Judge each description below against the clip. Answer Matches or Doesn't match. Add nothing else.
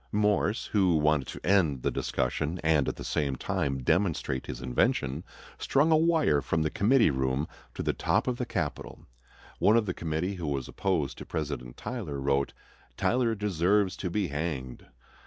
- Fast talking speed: Doesn't match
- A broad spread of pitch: Matches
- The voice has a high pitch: Doesn't match